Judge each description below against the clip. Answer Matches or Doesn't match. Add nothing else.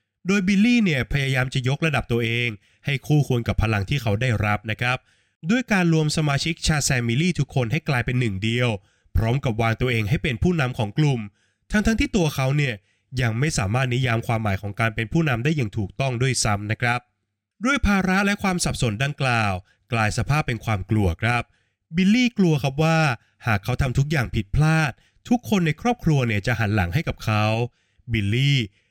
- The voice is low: Matches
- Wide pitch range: Matches